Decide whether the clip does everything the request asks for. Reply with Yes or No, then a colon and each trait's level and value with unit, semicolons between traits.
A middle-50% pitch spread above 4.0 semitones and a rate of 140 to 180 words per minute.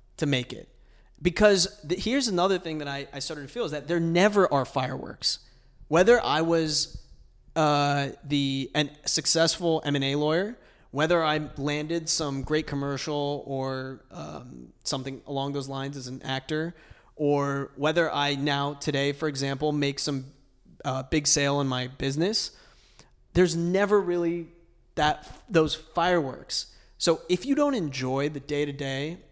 No: average, 3.3 semitones; average, 145 wpm